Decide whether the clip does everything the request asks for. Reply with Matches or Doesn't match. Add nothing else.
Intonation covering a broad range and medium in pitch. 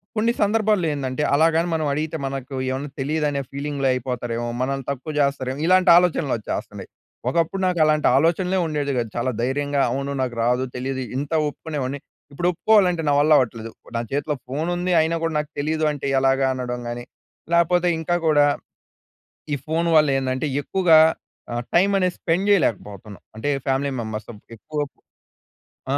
Doesn't match